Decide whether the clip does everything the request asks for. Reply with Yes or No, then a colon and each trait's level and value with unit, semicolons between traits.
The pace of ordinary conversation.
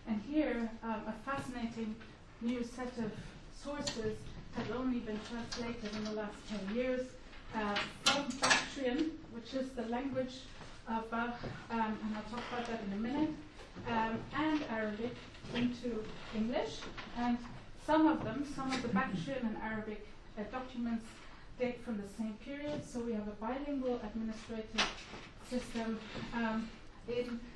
Yes: average, 150 wpm